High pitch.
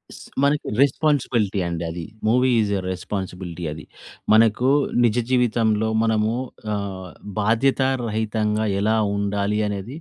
No: low, 110 Hz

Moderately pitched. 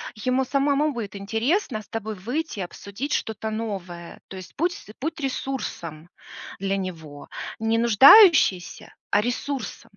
No: high, 225 Hz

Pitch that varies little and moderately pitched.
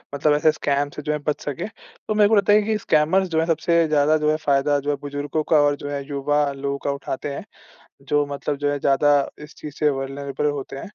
Yes: narrow, 1.7 semitones; medium, 145 Hz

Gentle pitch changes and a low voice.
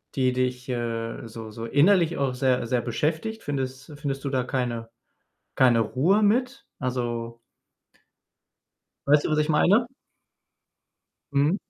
No: average, 4.2 semitones; low, 130 Hz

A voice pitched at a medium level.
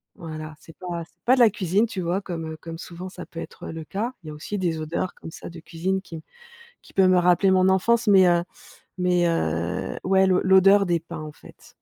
Yes: medium, 180 Hz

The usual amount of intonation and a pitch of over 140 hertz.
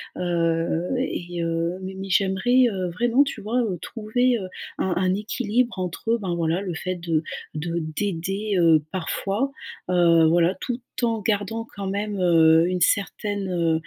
Yes: average, 3.9 semitones; high, 190 Hz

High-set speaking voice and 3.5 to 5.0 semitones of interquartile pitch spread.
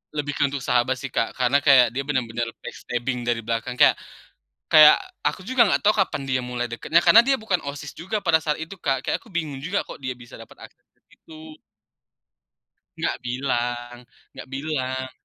No: low, 135 Hz; average, 4.3 semitones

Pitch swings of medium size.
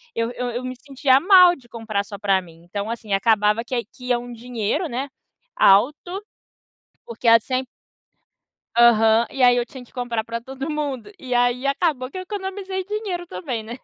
Yes: average, 3.9 semitones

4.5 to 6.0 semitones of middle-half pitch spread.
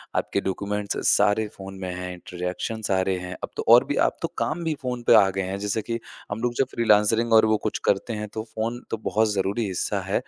No: average, 2.8 semitones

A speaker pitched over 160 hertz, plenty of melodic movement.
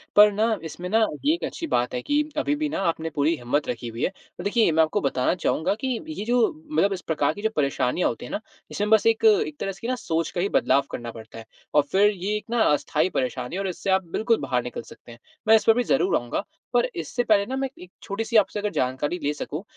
Yes: high, 190 Hz; wide, 7.8 semitones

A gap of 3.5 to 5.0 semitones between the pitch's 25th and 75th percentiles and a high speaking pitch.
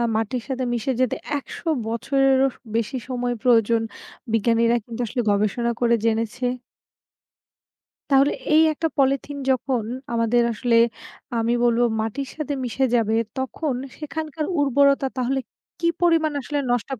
No: average, 3.1 semitones; very high, 250 Hz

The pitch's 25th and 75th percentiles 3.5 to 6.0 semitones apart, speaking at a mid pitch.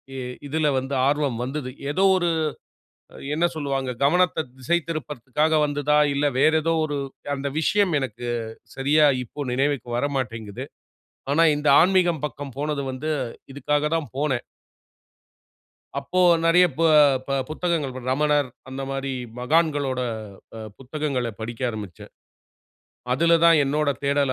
No: average, 2.9 semitones; medium, 145 Hz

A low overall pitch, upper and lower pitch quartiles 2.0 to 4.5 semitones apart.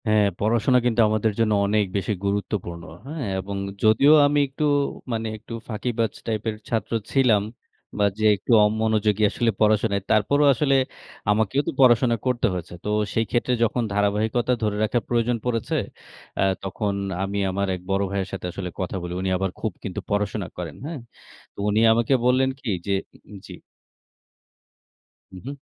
Yes: low, 110 Hz; average, 3.0 semitones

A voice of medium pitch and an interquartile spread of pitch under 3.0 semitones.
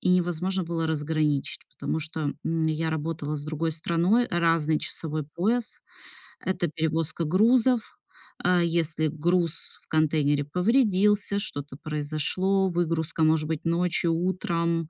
Yes: medium, 165 Hz; narrow, 2.6 semitones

